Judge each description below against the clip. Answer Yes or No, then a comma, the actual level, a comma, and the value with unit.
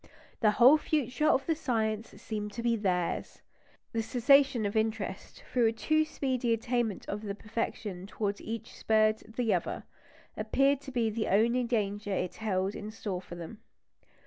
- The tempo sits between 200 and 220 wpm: No, average, 170 wpm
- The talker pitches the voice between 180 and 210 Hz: No, high, 225 Hz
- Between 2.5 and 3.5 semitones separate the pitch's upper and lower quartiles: Yes, average, 3.0 semitones